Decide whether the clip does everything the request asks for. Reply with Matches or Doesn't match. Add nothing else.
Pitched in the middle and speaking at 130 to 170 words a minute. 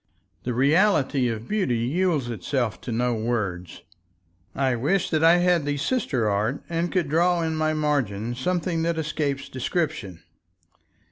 Matches